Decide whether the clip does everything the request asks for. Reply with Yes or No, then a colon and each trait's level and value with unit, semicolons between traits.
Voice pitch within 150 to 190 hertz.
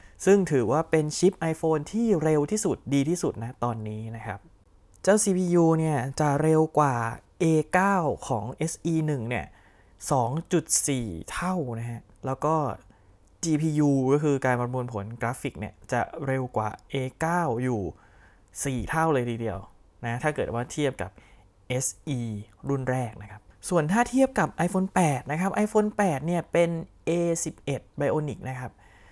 No: low, 135 Hz